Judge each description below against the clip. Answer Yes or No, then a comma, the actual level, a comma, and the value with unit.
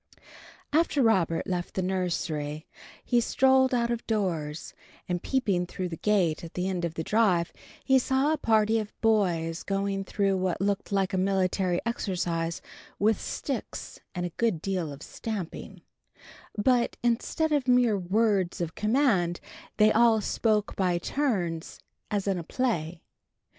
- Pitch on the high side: Yes, high, 195 Hz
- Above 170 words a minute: No, average, 155 wpm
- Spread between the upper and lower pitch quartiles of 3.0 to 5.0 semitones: Yes, average, 4.6 semitones